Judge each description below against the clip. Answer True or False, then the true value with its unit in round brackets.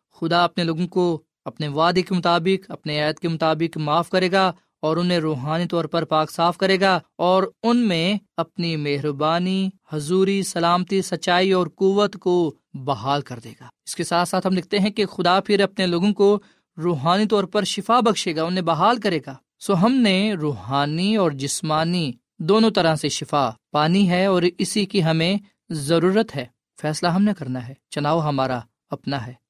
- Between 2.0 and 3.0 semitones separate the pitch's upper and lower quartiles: False (3.7 semitones)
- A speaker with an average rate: True (180 wpm)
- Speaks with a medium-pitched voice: True (175 Hz)